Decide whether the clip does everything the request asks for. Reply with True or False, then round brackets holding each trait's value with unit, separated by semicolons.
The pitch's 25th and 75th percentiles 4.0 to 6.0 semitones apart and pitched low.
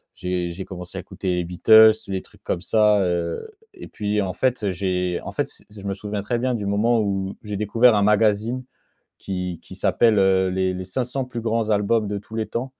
False (3.1 semitones; 105 Hz)